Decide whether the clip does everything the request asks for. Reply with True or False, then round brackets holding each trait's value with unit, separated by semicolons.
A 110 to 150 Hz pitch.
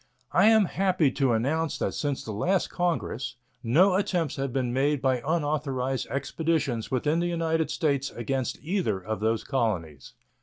True (140 Hz)